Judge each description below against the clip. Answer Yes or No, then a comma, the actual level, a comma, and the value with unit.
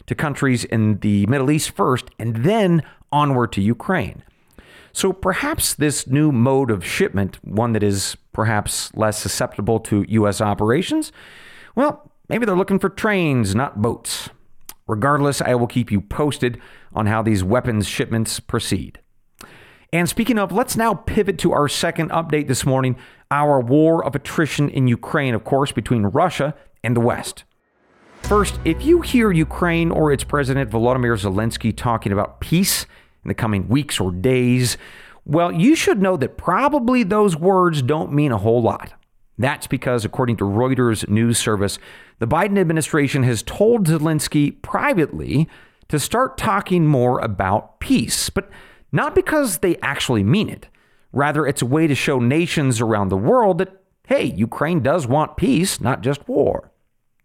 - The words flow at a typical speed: Yes, average, 160 wpm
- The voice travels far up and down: Yes, wide, 6.3 semitones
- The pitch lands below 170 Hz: Yes, low, 135 Hz